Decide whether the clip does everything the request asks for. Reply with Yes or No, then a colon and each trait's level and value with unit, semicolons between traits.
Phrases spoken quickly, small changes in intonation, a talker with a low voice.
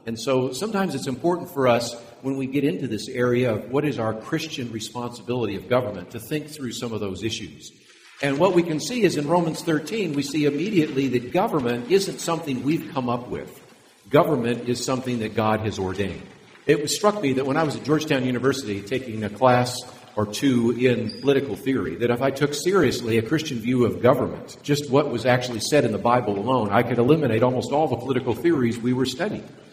No: fast, 210 wpm; average, 3.6 semitones; low, 125 Hz